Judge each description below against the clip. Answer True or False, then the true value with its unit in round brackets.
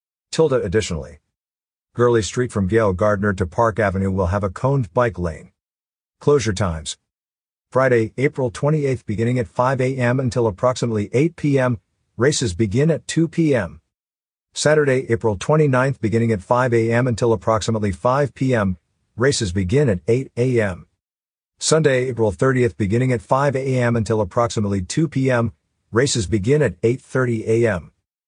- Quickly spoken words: False (140 wpm)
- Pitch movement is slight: False (3.8 semitones)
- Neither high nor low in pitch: False (115 Hz)